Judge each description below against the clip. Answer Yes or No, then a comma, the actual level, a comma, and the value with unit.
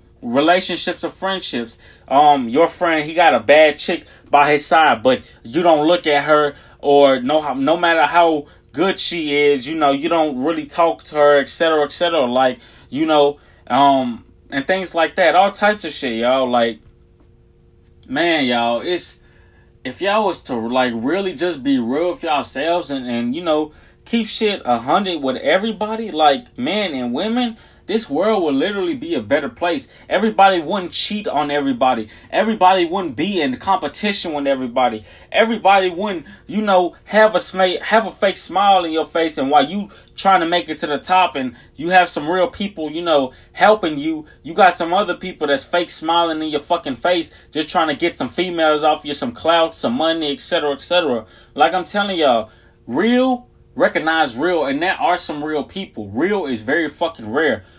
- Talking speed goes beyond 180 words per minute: Yes, average, 190 wpm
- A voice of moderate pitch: Yes, medium, 165 Hz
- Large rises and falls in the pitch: No, average, 4.8 semitones